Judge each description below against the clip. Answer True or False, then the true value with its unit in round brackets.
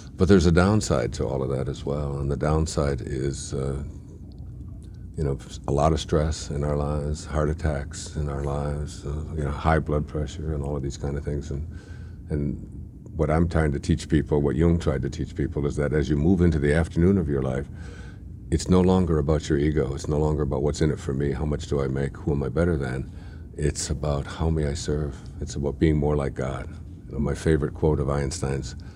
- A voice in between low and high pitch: False (75 Hz)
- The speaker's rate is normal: False (230 wpm)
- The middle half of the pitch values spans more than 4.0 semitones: False (2.9 semitones)